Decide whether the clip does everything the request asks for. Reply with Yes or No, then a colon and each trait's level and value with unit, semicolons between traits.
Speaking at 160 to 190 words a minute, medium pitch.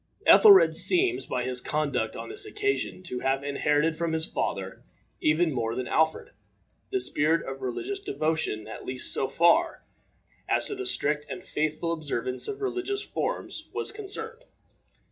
No: average, 150 wpm; medium, 160 Hz